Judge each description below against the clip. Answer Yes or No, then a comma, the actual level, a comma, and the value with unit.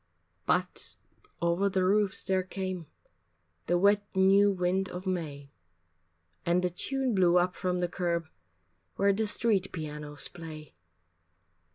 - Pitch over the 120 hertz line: Yes, medium, 185 Hz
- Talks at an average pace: No, slow, 130 wpm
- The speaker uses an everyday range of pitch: No, narrow, 2.2 semitones